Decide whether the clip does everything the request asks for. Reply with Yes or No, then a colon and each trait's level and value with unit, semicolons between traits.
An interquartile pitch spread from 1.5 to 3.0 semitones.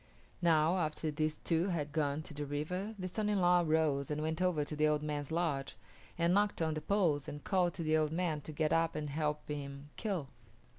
Yes: average, 2.7 semitones